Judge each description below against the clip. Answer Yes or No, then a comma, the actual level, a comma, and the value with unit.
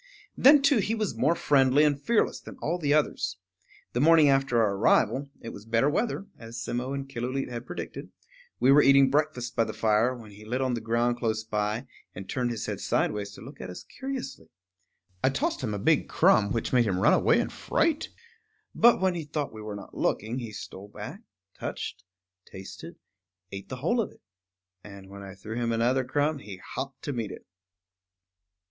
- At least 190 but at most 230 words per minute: Yes, average, 200 wpm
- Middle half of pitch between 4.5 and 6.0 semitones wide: Yes, average, 5.0 semitones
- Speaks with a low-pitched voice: Yes, low, 125 Hz